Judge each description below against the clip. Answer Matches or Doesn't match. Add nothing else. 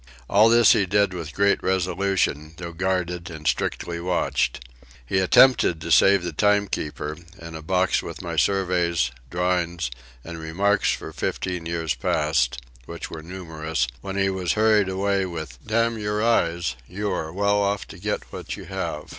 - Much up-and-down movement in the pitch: Doesn't match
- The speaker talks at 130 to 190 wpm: Matches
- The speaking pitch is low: Matches